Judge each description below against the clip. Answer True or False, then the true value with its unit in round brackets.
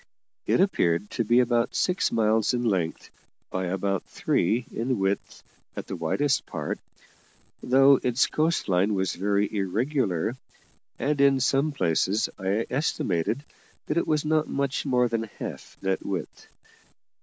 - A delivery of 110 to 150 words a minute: True (145 wpm)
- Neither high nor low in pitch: False (115 Hz)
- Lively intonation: True (5.9 semitones)